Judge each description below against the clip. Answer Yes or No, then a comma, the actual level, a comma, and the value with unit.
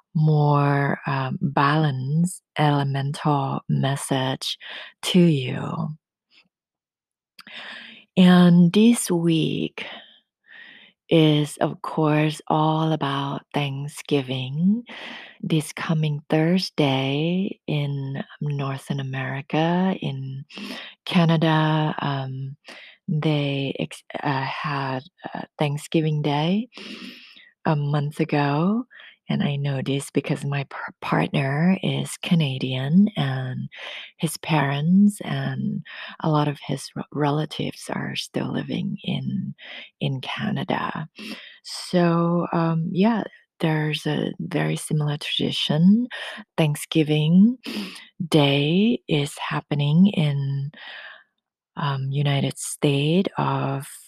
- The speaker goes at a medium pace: No, slow, 85 wpm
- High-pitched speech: No, medium, 155 Hz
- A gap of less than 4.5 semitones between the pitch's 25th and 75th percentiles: Yes, average, 3.8 semitones